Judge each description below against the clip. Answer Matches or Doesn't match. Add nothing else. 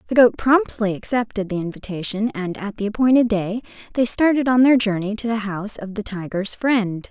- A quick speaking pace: Doesn't match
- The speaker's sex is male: Doesn't match